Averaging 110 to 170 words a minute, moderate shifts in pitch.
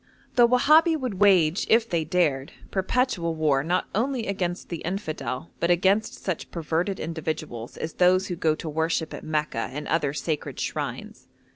Yes: average, 160 wpm; average, 4.1 semitones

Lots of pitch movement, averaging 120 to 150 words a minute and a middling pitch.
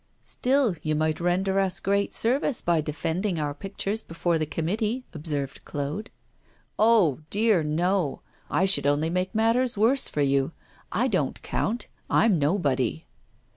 Yes: wide, 5.8 semitones; average, 140 wpm; medium, 180 Hz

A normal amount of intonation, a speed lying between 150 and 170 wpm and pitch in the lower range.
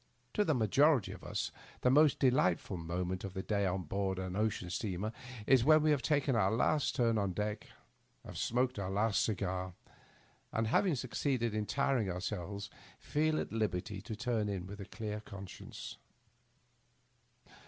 Yes: average, 4.9 semitones; average, 165 wpm; low, 105 Hz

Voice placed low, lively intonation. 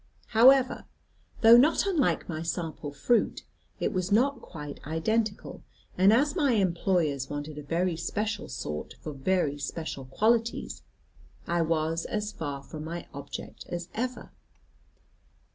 No: medium, 175 Hz; wide, 6.5 semitones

